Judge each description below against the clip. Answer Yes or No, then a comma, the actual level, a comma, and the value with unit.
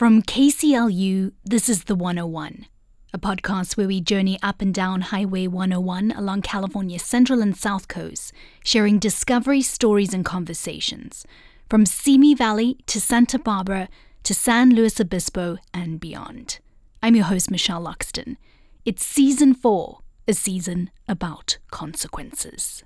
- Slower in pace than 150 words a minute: Yes, slow, 135 wpm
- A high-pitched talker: Yes, high, 200 Hz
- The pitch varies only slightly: No, average, 3.7 semitones